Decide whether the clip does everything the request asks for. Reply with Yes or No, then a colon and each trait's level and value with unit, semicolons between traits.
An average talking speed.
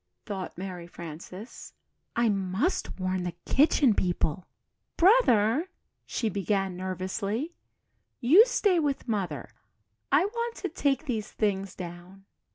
No: slow, 115 wpm